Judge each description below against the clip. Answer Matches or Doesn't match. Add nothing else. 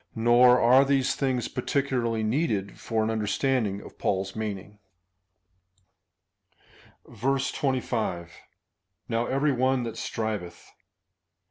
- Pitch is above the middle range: Doesn't match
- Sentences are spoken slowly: Matches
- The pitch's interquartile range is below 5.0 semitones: Matches